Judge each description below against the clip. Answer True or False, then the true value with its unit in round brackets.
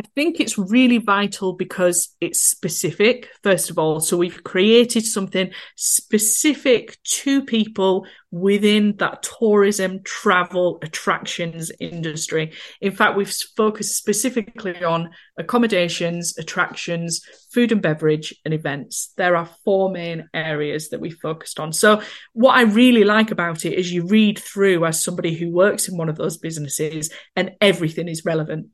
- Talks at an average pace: True (145 wpm)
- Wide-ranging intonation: False (4.1 semitones)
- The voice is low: False (185 Hz)